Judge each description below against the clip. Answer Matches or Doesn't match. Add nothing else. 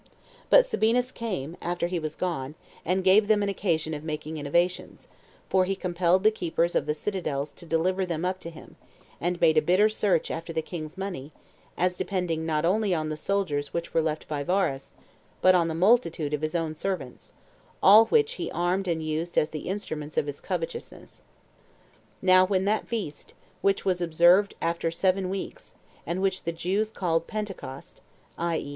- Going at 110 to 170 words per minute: Doesn't match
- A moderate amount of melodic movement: Matches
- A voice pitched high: Doesn't match